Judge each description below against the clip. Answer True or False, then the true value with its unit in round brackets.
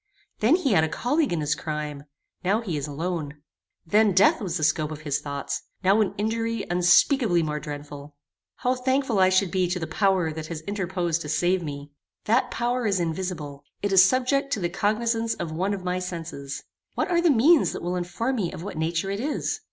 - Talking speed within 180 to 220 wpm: True (205 wpm)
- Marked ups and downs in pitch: True (5.9 semitones)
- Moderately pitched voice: True (180 Hz)